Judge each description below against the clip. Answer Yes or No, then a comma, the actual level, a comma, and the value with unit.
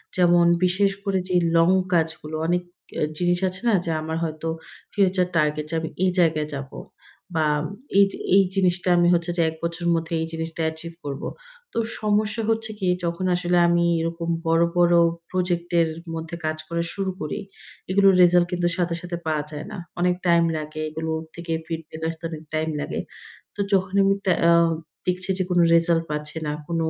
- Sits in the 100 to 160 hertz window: No, medium, 170 Hz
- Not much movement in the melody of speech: Yes, narrow, 2.0 semitones